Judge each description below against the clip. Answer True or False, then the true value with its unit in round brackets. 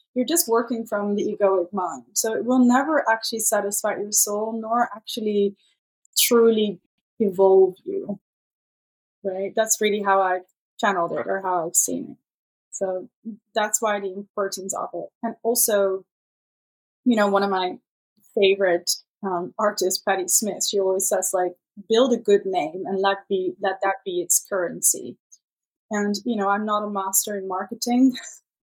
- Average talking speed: True (160 wpm)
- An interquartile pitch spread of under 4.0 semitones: True (2.7 semitones)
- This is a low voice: False (205 Hz)